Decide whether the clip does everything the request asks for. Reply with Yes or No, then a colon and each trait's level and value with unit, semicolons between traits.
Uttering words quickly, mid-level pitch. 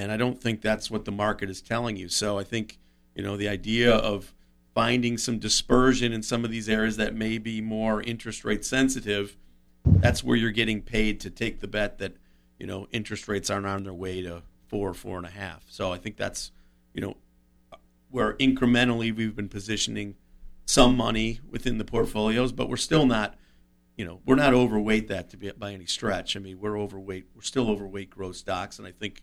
No: fast, 210 wpm; low, 105 Hz